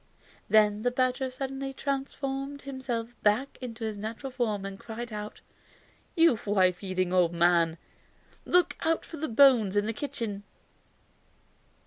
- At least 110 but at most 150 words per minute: Yes, slow, 135 wpm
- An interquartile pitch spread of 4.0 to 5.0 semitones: Yes, average, 4.7 semitones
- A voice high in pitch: Yes, high, 230 Hz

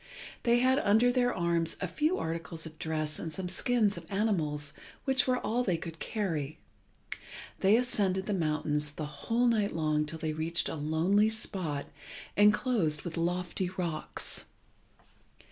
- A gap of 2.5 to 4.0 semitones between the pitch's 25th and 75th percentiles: No, average, 5.3 semitones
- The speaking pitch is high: No, medium, 175 Hz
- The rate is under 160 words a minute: Yes, average, 150 wpm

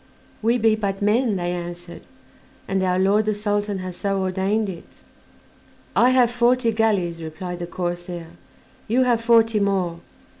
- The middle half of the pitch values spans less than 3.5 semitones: No, average, 3.9 semitones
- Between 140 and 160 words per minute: Yes, average, 150 wpm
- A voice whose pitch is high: Yes, high, 200 Hz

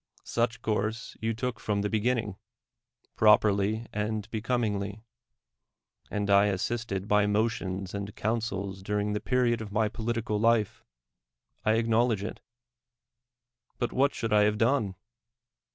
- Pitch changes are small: Yes, narrow, 2.1 semitones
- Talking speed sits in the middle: No, slow, 130 wpm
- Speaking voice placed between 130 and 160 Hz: No, low, 105 Hz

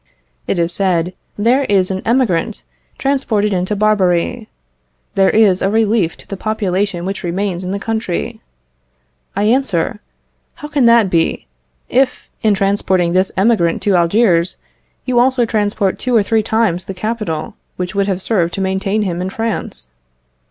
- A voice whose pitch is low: No, high, 200 Hz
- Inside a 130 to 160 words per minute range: Yes, average, 155 wpm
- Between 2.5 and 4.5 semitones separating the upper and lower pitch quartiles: Yes, average, 3.4 semitones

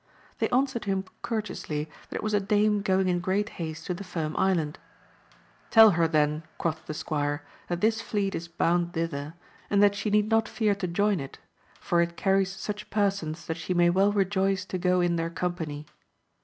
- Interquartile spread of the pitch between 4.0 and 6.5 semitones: No, average, 3.6 semitones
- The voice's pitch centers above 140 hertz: Yes, medium, 185 Hz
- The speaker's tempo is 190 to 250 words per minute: Yes, average, 195 wpm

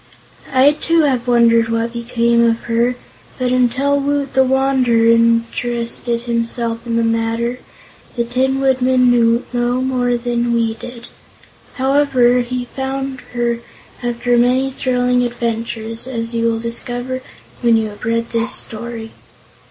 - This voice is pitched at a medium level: No, high, 240 Hz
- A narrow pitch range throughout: Yes, narrow, 1.7 semitones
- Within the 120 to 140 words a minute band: Yes, slow, 135 wpm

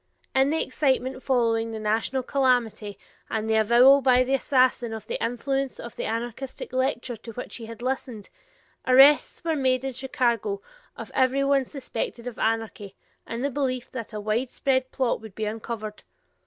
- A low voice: No, very high, 250 Hz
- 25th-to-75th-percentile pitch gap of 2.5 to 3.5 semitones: Yes, average, 2.9 semitones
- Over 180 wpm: No, average, 170 wpm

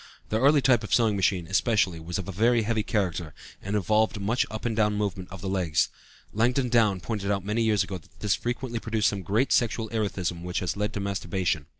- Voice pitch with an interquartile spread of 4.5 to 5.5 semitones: No, average, 3.0 semitones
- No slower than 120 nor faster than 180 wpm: No, fast, 205 wpm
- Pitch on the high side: No, low, 105 Hz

